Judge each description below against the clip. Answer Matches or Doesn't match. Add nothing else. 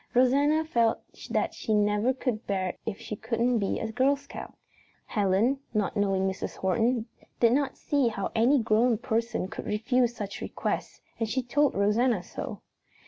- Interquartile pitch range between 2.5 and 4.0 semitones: Matches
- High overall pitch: Matches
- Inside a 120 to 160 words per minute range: Doesn't match